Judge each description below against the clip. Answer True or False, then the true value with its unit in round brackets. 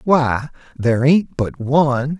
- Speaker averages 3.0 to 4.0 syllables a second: True (3.8 syllables/s)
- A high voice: False (140 Hz)